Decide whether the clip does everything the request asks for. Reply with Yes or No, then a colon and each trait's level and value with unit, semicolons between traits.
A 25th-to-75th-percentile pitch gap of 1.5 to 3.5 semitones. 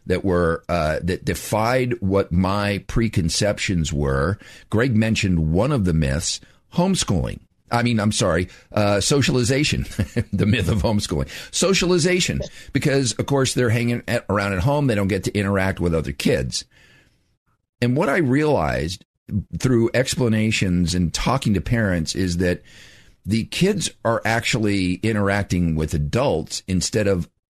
No: average, 5.0 semitones